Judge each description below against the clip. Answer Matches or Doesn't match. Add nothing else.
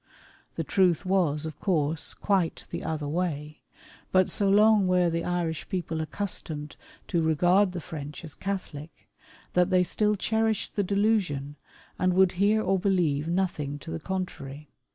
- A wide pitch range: Doesn't match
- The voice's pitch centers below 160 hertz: Doesn't match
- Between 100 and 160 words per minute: Matches